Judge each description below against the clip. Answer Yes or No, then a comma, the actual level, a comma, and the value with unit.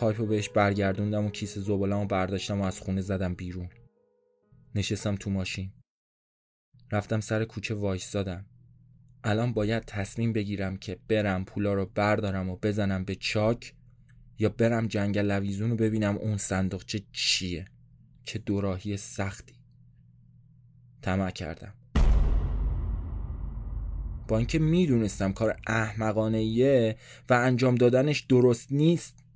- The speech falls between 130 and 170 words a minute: No, average, 120 wpm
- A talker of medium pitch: No, low, 105 Hz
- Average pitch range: Yes, average, 4.0 semitones